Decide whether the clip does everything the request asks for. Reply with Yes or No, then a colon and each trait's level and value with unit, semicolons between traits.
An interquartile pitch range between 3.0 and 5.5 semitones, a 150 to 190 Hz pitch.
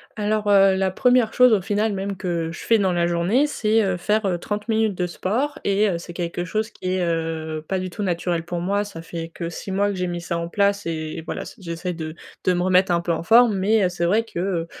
Yes: average, 3.4 semitones; medium, 185 Hz